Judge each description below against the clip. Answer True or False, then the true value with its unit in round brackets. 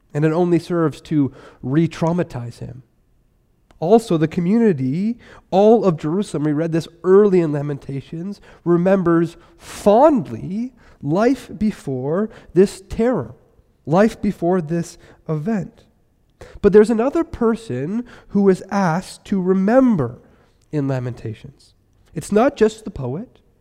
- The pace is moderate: False (115 wpm)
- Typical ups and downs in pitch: False (6.1 semitones)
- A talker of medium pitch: True (175 Hz)